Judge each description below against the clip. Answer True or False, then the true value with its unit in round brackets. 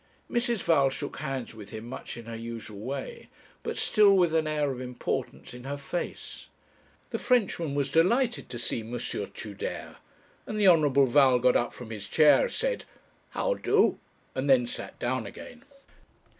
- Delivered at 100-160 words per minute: False (170 wpm)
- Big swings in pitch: True (6.2 semitones)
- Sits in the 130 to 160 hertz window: True (140 Hz)